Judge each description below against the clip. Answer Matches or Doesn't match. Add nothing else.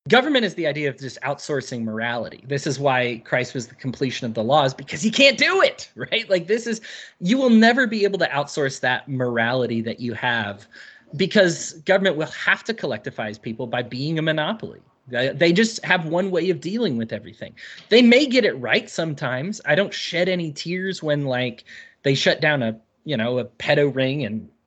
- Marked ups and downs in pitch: Matches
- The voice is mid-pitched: Matches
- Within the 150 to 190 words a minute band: Doesn't match